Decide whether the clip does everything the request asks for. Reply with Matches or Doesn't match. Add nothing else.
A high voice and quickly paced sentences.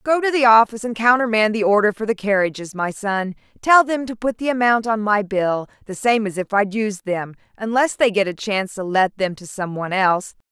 Matches